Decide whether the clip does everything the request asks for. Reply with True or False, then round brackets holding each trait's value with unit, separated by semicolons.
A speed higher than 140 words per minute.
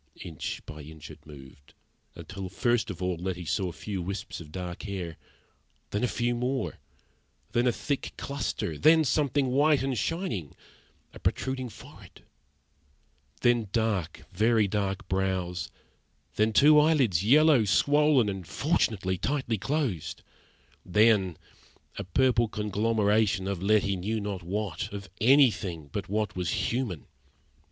False (135 wpm)